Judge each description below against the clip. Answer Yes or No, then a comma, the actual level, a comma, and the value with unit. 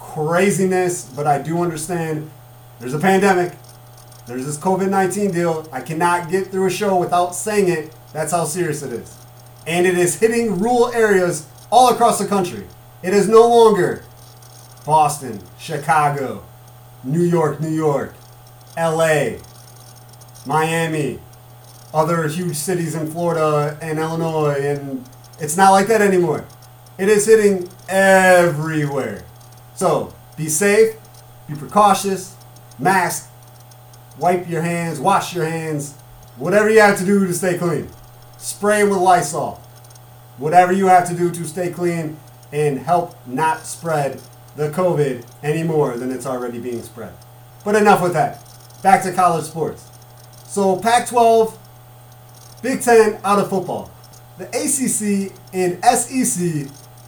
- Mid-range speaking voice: Yes, medium, 155 Hz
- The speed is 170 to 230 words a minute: No, slow, 135 wpm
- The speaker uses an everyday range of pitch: No, wide, 7.1 semitones